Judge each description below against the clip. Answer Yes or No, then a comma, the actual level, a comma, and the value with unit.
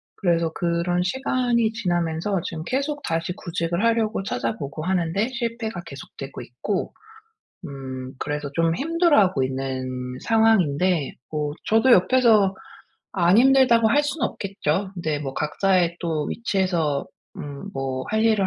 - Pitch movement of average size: No, wide, 6.6 semitones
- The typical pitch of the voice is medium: Yes, medium, 180 Hz